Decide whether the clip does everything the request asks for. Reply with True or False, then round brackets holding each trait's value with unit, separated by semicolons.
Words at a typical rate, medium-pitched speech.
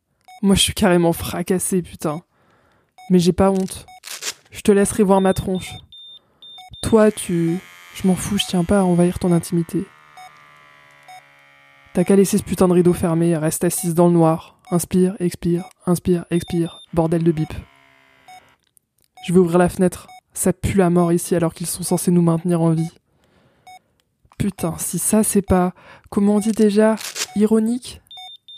True (160 wpm; 180 Hz)